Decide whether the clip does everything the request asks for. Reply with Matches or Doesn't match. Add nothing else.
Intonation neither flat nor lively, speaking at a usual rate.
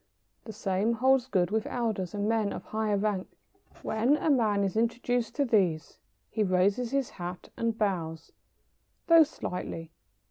Matches